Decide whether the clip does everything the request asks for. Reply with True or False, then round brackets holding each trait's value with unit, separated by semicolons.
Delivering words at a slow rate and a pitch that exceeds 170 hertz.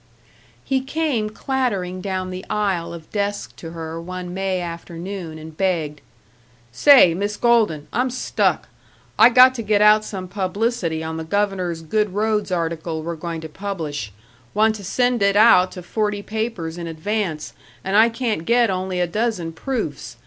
False (170 wpm; 190 Hz)